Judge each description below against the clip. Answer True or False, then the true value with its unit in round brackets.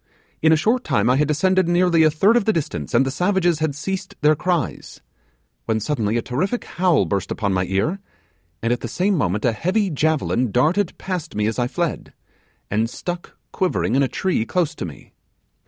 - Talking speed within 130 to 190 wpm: False (200 wpm)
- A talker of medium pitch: True (155 Hz)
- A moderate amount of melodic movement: False (7.4 semitones)